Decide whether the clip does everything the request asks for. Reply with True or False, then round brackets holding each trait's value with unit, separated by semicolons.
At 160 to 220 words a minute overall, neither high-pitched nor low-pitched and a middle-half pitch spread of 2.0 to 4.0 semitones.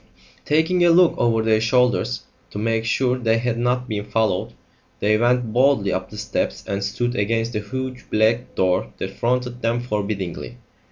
False (170 wpm; 115 Hz; 2.9 semitones)